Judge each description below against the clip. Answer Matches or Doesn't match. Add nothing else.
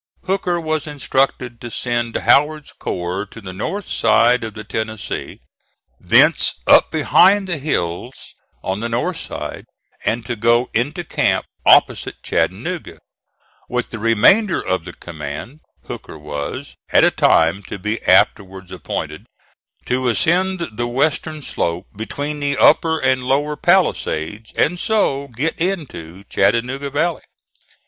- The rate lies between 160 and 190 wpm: Doesn't match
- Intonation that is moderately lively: Doesn't match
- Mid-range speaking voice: Doesn't match